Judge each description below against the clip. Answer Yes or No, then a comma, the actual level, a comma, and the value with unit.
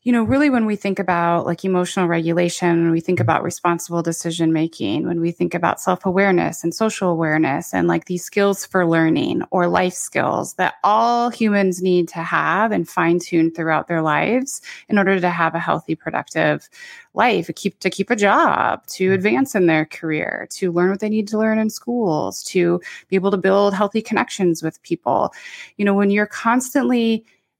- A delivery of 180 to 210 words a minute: Yes, average, 190 wpm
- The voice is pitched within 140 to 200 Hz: Yes, medium, 185 Hz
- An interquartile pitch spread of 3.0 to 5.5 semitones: Yes, average, 3.9 semitones